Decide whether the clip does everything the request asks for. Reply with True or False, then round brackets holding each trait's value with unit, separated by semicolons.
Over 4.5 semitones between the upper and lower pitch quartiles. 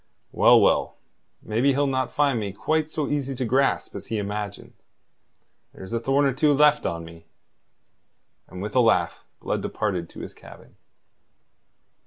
True (5.6 semitones)